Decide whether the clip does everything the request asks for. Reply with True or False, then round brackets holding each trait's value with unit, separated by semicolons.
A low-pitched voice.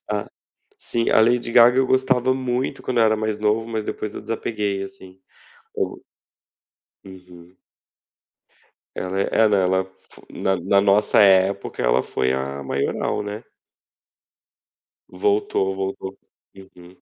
True (100 Hz)